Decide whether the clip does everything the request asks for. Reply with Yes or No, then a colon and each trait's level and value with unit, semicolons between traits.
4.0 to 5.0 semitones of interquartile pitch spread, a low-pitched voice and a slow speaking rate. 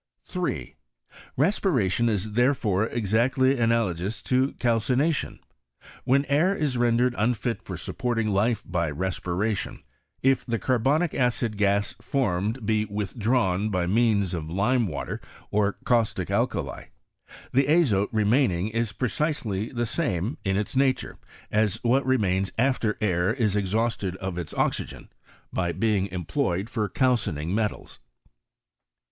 Yes: average, 4.4 semitones; low, 110 Hz; slow, 130 wpm